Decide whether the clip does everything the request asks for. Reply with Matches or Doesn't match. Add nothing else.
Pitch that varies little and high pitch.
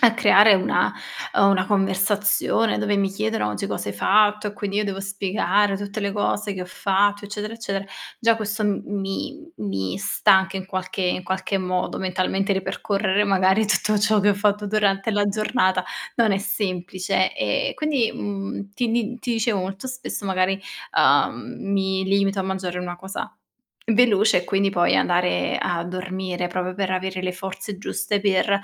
Matches